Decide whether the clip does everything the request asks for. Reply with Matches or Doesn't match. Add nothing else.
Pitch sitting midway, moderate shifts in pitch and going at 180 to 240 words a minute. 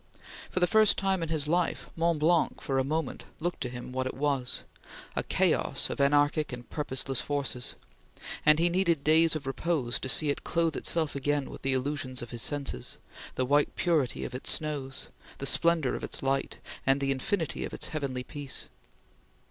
Matches